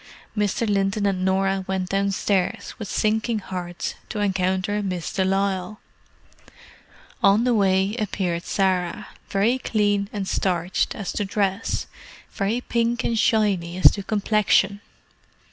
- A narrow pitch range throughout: Yes, narrow, 1.9 semitones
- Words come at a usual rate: No, slow, 130 wpm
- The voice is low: No, high, 195 Hz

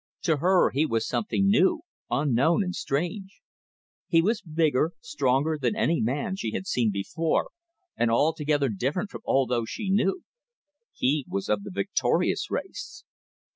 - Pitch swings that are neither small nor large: No, wide, 6.6 semitones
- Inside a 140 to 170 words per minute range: Yes, average, 150 wpm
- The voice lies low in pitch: No, medium, 155 Hz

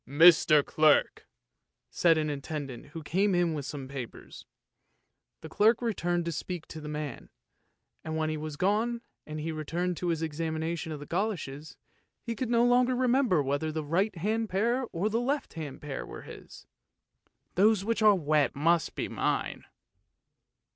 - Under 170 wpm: No, average, 175 wpm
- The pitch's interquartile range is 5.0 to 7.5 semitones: Yes, wide, 5.6 semitones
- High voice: No, medium, 165 Hz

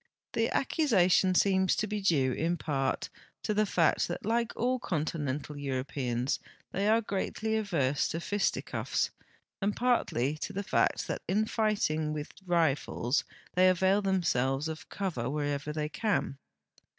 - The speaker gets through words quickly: No, average, 140 wpm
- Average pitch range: No, wide, 6.0 semitones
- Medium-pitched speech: Yes, medium, 175 Hz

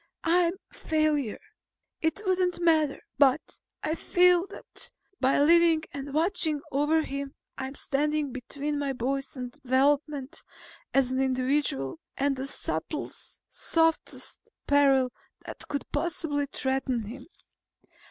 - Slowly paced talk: Yes, slow, 115 wpm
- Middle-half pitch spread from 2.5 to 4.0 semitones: Yes, average, 3.0 semitones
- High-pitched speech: Yes, very high, 285 Hz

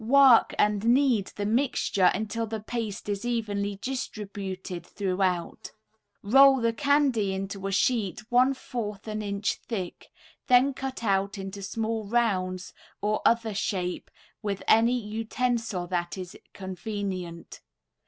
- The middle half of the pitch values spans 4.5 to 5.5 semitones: No, average, 3.3 semitones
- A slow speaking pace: Yes, slow, 125 wpm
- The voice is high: Yes, high, 210 Hz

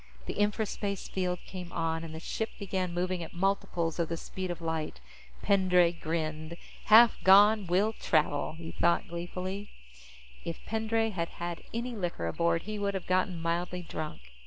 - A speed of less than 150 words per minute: No, average, 160 wpm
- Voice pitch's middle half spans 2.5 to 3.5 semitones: Yes, average, 3.1 semitones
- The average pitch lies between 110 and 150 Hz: No, medium, 180 Hz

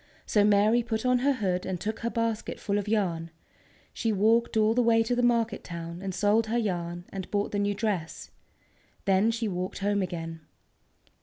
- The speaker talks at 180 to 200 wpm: Yes, average, 190 wpm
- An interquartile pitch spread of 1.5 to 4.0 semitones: Yes, average, 3.4 semitones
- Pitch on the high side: Yes, high, 205 Hz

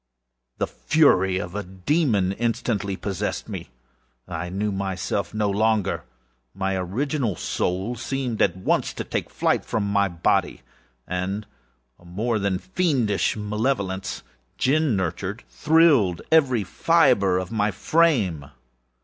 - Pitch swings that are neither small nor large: Yes, average, 4.6 semitones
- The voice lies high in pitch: No, low, 100 Hz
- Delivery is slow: Yes, slow, 125 wpm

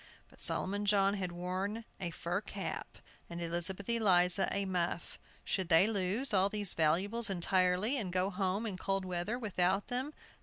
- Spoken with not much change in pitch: Yes, narrow, 2.3 semitones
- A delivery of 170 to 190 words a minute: No, average, 160 wpm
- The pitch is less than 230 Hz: Yes, high, 190 Hz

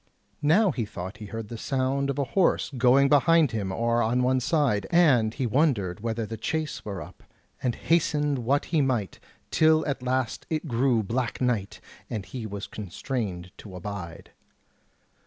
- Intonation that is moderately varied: Yes, average, 4.8 semitones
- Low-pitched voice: Yes, low, 125 Hz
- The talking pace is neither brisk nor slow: Yes, average, 170 wpm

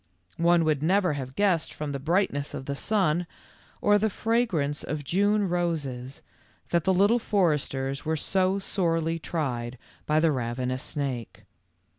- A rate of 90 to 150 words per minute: Yes, average, 145 wpm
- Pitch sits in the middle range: Yes, medium, 160 Hz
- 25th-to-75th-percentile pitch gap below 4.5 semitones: No, average, 5.2 semitones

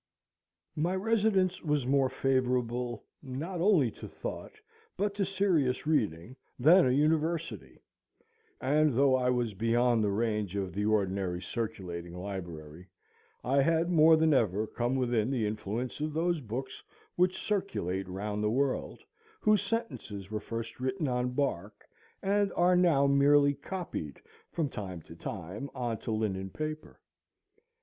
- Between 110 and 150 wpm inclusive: Yes, average, 140 wpm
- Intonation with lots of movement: Yes, wide, 7.0 semitones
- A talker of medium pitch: No, low, 125 Hz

